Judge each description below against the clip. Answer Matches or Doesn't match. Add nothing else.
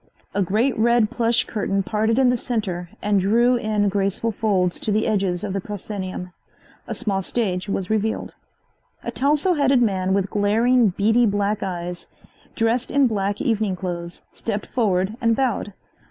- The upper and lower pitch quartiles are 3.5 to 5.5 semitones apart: Doesn't match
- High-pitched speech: Matches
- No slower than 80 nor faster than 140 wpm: Doesn't match